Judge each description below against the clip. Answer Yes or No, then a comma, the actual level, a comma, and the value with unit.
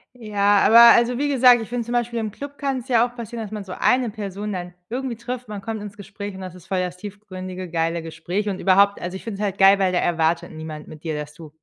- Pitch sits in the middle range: No, high, 200 Hz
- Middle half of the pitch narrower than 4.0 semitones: No, average, 4.3 semitones